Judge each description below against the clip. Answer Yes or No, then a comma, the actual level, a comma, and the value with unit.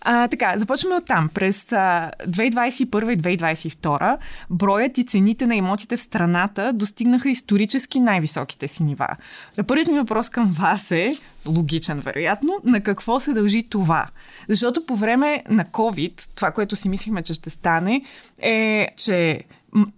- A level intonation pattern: No, average, 5.2 semitones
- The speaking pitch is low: No, high, 210 Hz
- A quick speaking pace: No, average, 150 wpm